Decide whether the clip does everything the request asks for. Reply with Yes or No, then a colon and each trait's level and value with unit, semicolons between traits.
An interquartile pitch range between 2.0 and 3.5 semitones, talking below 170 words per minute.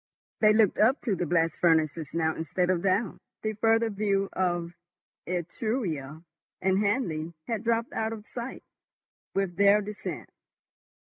No: average, 4.4 semitones; average, 140 wpm